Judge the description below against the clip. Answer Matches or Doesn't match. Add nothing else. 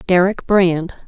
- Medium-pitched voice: Matches